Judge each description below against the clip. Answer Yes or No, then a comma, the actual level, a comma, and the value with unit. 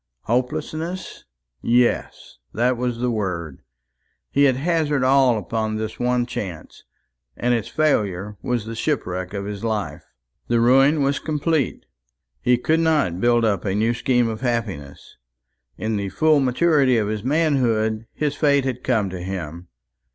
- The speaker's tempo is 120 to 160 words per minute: Yes, average, 150 wpm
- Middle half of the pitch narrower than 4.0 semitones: No, average, 4.6 semitones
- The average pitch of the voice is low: Yes, low, 120 Hz